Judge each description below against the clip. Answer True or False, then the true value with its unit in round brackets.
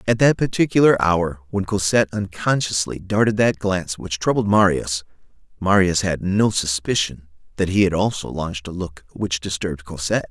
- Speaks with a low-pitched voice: True (95 Hz)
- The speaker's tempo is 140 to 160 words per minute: True (155 wpm)